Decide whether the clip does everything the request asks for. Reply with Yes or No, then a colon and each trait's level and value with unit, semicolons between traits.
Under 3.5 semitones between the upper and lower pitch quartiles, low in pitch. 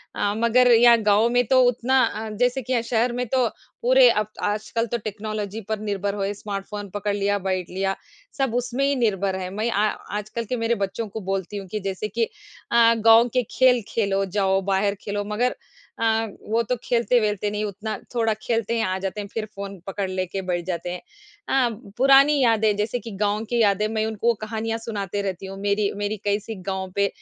No: average, 2.7 semitones; high, 215 Hz